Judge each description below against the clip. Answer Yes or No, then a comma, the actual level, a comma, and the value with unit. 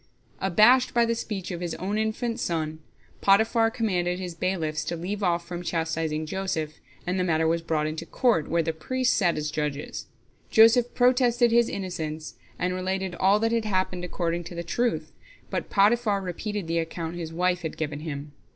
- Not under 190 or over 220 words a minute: No, average, 180 wpm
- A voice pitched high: No, medium, 180 Hz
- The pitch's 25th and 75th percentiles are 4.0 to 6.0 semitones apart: Yes, average, 4.7 semitones